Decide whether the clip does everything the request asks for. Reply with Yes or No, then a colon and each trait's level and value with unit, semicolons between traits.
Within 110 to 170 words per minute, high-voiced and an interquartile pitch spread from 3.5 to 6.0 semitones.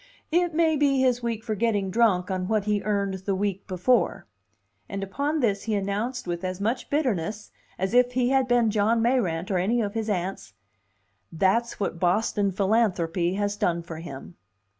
No: average, 180 wpm; high, 205 Hz; average, 4.1 semitones